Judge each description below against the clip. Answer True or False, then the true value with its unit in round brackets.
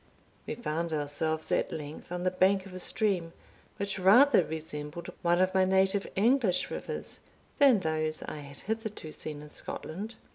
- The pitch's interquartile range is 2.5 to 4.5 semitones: True (3.9 semitones)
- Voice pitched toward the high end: False (180 Hz)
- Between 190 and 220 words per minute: False (160 wpm)